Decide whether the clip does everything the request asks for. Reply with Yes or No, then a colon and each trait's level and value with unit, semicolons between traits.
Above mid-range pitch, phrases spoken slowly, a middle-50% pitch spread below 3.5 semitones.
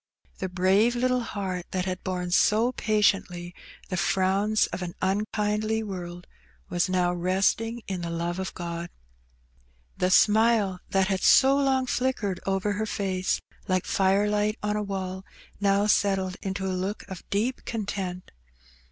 No: high, 195 Hz; average, 145 wpm; narrow, 2.4 semitones